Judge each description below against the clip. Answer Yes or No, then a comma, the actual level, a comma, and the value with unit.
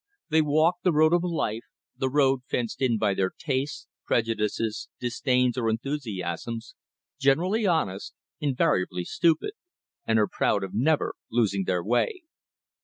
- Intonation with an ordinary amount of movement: No, wide, 6.2 semitones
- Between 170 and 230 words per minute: No, slow, 135 wpm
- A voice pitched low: Yes, low, 125 Hz